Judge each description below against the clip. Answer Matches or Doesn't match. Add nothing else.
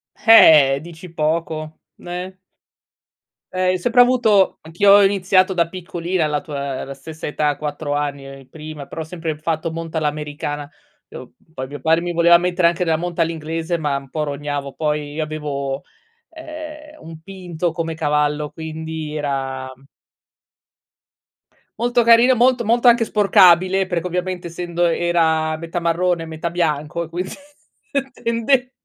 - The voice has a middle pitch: Matches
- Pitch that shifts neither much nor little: Matches